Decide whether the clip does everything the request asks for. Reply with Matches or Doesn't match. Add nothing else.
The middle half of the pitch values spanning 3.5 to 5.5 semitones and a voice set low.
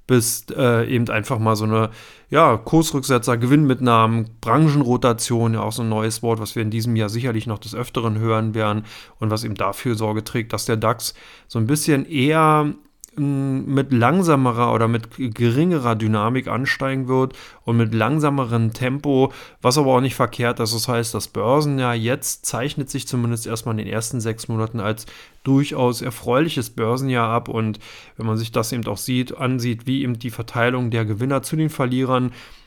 Doesn't match